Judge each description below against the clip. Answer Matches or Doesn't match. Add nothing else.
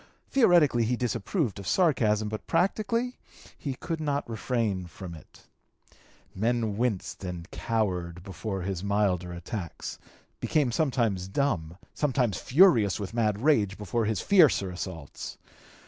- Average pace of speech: Doesn't match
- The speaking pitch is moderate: Doesn't match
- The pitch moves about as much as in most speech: Doesn't match